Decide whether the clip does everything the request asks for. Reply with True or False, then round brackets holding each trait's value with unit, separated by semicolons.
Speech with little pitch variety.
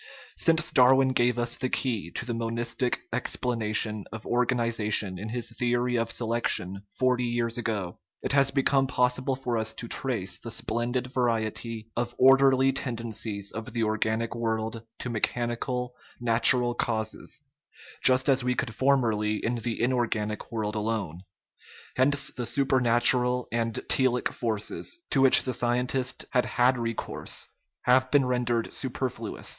True (2.2 semitones)